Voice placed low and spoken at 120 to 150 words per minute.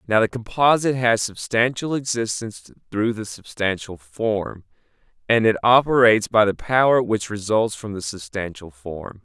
Yes: low, 110 Hz; average, 145 wpm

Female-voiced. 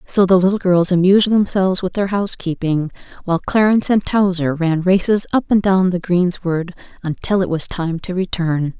Yes: female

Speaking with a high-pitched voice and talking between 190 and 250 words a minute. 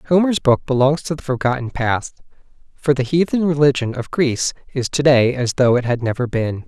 No: low, 135 Hz; average, 200 wpm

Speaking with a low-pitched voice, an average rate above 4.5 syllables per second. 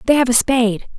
No: high, 245 Hz; 6.6 syllables/s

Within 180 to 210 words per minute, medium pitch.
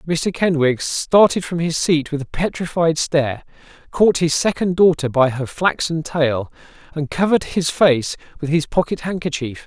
No: average, 160 wpm; medium, 160 Hz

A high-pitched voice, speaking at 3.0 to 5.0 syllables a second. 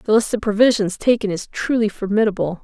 No: high, 210 Hz; 5.8 syllables/s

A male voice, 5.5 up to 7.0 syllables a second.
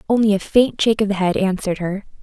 No: female; 6.8 syllables/s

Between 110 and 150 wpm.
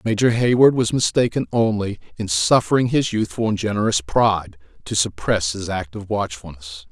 Yes: average, 145 wpm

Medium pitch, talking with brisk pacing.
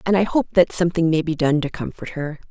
Yes: medium, 165 Hz; fast, 265 wpm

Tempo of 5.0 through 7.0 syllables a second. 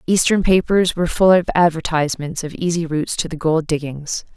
Yes: 5.6 syllables/s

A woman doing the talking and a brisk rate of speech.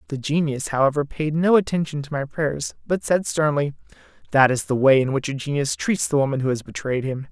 No: male; fast, 220 wpm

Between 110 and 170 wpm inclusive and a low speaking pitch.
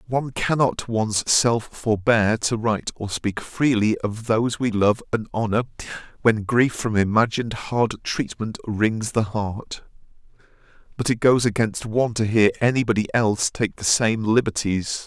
Yes: average, 155 wpm; low, 110 Hz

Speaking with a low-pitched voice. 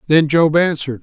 No: medium, 155 Hz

